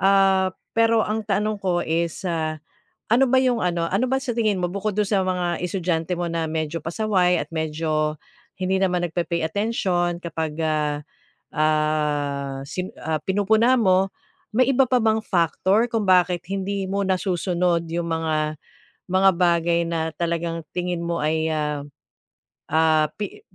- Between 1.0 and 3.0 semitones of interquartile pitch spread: No, average, 3.4 semitones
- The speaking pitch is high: No, medium, 175 Hz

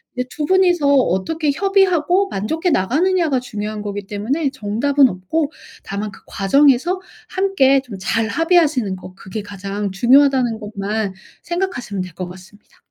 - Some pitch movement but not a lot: No, wide, 7.9 semitones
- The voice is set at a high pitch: Yes, very high, 250 Hz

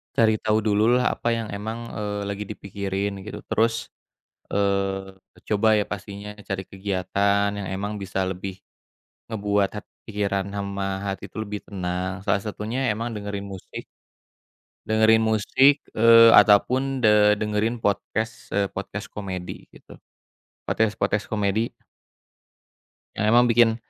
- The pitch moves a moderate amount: No, narrow, 2.0 semitones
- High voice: No, low, 105 Hz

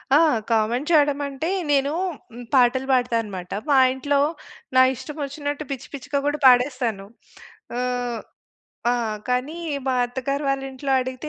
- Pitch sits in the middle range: No, very high, 265 Hz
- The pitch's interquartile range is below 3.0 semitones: Yes, narrow, 2.5 semitones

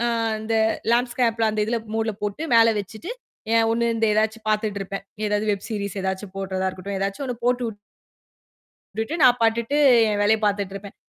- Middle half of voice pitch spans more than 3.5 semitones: No, narrow, 2.4 semitones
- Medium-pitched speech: No, high, 215 Hz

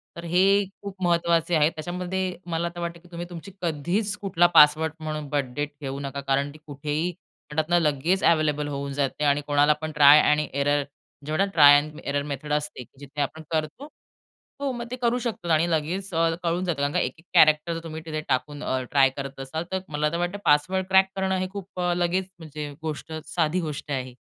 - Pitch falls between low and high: Yes, medium, 155 Hz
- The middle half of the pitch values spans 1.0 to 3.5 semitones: Yes, average, 3.2 semitones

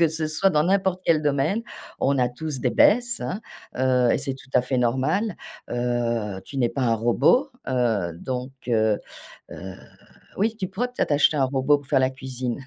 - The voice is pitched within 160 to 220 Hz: No, low, 135 Hz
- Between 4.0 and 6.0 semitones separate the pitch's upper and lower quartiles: Yes, average, 4.6 semitones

